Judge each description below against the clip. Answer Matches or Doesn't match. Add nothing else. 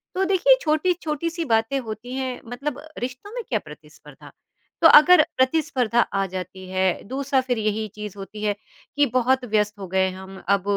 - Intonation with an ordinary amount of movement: Doesn't match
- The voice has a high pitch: Matches